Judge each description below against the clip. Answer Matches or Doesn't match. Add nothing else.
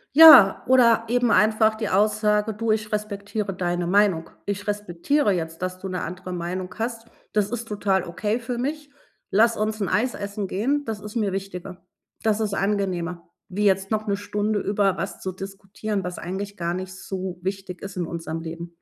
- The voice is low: Doesn't match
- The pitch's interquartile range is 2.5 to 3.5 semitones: Matches